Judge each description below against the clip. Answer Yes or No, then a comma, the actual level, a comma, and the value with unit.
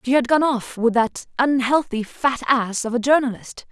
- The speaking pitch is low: No, very high, 250 Hz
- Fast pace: No, average, 180 wpm